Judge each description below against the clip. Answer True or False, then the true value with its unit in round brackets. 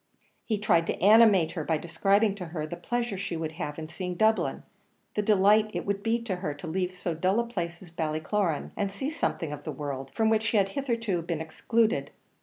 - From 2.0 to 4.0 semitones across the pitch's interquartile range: False (4.8 semitones)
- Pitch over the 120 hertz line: True (190 Hz)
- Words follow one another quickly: True (215 wpm)